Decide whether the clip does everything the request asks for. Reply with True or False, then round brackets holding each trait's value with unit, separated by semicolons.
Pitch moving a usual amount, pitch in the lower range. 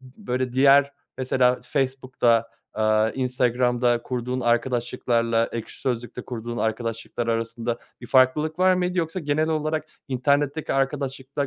True (3.0 semitones; 125 Hz)